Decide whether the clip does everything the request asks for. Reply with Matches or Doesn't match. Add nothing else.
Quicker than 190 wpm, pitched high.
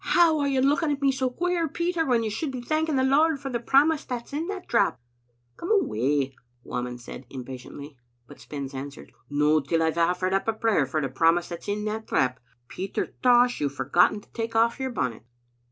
Matches